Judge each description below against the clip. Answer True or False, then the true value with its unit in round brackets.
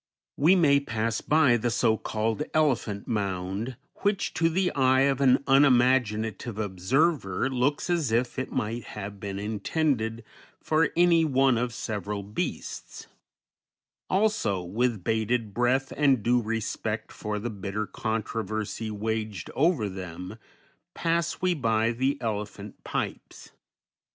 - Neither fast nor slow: False (130 wpm)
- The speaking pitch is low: True (115 Hz)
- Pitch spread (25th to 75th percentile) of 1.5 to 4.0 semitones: False (4.5 semitones)